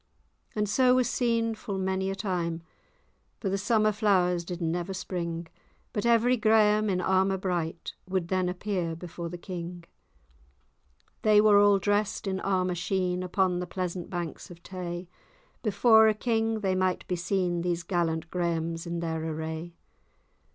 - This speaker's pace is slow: No, average, 155 wpm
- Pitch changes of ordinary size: Yes, average, 3.1 semitones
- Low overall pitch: No, medium, 185 Hz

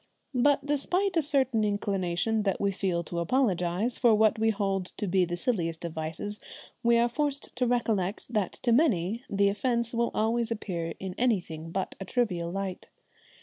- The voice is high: Yes, high, 210 Hz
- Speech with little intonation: No, average, 4.7 semitones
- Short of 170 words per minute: No, average, 175 wpm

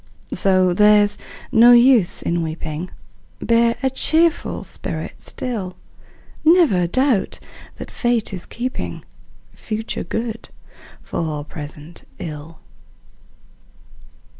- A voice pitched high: Yes, high, 205 Hz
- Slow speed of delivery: Yes, slow, 90 wpm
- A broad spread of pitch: Yes, wide, 6.1 semitones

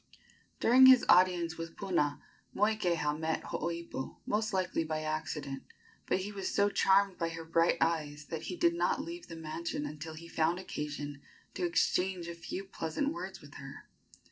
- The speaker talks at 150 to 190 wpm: Yes, average, 170 wpm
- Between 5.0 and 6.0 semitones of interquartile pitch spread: No, average, 3.4 semitones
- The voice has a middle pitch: Yes, medium, 170 Hz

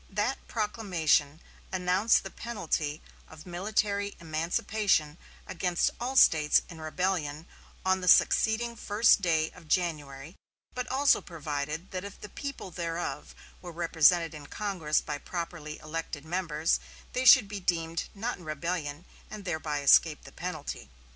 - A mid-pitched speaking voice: Yes, medium, 175 Hz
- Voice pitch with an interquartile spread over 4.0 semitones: Yes, average, 4.4 semitones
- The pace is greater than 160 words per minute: No, slow, 135 wpm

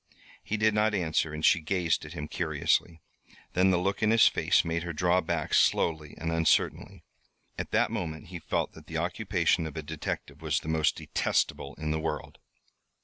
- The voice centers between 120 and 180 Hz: No, very low, 80 Hz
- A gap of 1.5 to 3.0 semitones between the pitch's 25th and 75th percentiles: Yes, average, 2.7 semitones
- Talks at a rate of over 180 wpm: Yes, average, 190 wpm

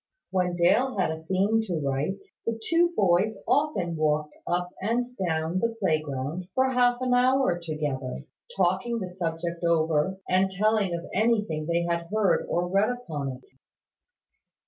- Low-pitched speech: No, medium, 180 Hz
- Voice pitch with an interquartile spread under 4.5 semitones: No, average, 5.3 semitones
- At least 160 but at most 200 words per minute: No, average, 150 wpm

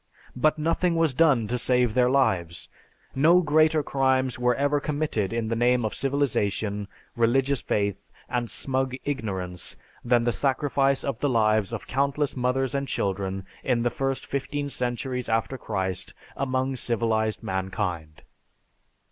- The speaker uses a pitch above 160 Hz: No, low, 125 Hz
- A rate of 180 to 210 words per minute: No, average, 140 wpm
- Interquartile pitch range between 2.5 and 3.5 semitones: No, average, 4.0 semitones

